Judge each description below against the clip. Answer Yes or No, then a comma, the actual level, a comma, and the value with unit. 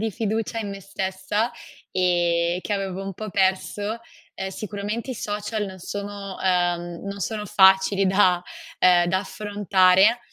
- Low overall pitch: No, high, 195 Hz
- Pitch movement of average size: No, narrow, 2.1 semitones